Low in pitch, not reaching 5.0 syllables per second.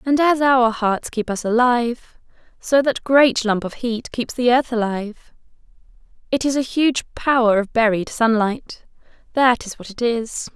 No: high, 240 Hz; 4.4 syllables/s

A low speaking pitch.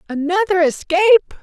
No: very high, 360 Hz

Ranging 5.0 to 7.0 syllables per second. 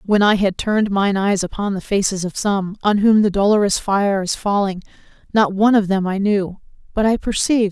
Yes: 5.3 syllables/s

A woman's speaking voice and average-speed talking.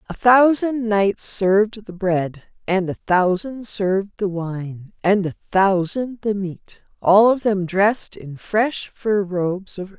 Yes: female; average, 155 wpm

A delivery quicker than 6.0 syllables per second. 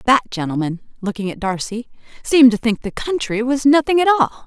Yes: 6.3 syllables/s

